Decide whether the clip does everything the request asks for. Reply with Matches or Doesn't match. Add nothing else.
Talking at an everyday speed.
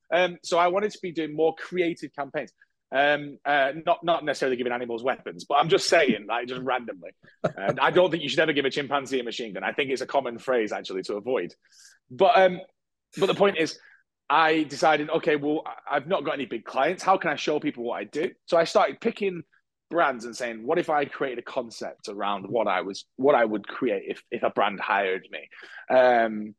Doesn't match